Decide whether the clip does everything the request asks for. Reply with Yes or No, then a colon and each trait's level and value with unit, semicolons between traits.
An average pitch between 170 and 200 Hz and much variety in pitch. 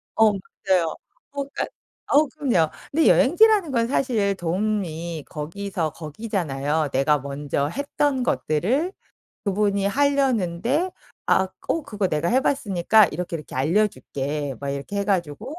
Yes: high, 195 Hz; wide, 8.4 semitones